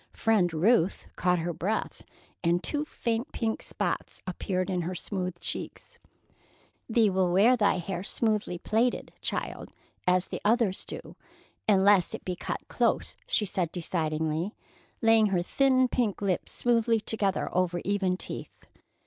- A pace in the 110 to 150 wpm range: Yes, average, 140 wpm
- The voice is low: No, high, 195 Hz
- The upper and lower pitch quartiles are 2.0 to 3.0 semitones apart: No, average, 3.9 semitones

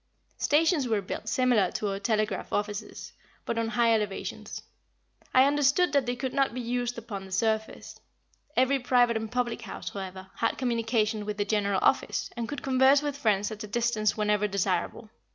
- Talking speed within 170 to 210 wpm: Yes, average, 175 wpm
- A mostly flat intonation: No, average, 3.2 semitones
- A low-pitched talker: No, high, 230 Hz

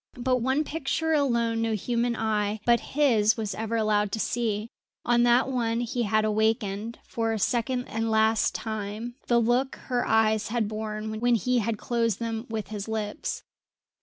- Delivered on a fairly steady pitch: Yes, narrow, 1.9 semitones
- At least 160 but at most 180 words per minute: Yes, average, 170 wpm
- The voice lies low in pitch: No, high, 225 Hz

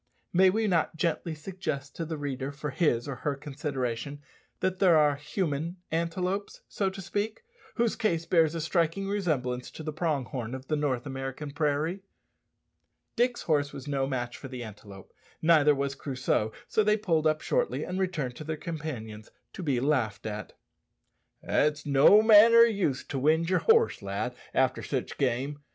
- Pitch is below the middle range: No, medium, 150 Hz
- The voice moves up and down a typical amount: Yes, average, 5.0 semitones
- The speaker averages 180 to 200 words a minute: No, average, 170 wpm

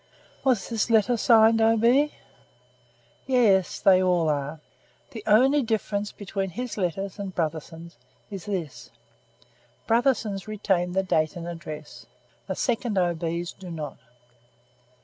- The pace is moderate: No, slow, 130 wpm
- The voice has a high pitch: Yes, high, 195 Hz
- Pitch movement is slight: No, average, 4.6 semitones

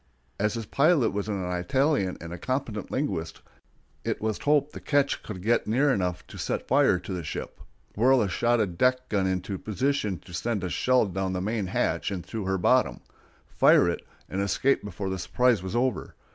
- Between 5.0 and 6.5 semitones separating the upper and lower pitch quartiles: Yes, wide, 5.4 semitones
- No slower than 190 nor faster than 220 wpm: Yes, average, 195 wpm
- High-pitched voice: No, low, 105 Hz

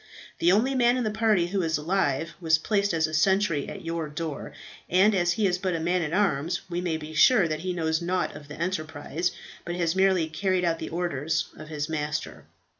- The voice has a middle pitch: Yes, medium, 170 Hz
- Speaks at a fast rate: Yes, fast, 220 wpm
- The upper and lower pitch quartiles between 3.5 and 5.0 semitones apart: No, average, 3.1 semitones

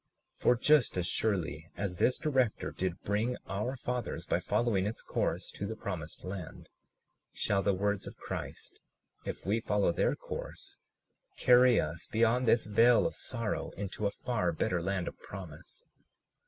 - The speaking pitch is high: No, low, 105 Hz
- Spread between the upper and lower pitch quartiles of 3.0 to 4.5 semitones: Yes, average, 4.2 semitones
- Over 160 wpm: No, average, 155 wpm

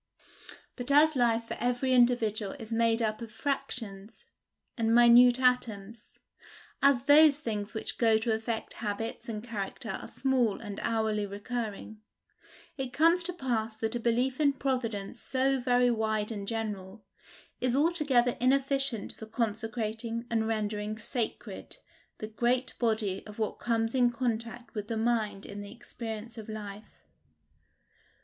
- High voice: Yes, high, 230 Hz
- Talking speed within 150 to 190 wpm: No, average, 140 wpm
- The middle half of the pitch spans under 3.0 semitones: Yes, narrow, 2.4 semitones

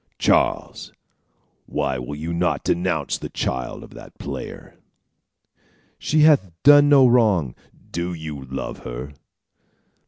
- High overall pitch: No, very low, 85 Hz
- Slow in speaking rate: Yes, slow, 120 wpm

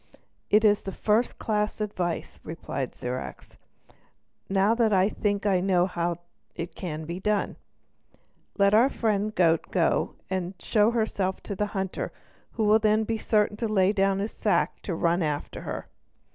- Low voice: No, high, 200 Hz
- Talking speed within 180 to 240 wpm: No, average, 160 wpm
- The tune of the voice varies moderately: Yes, average, 3.0 semitones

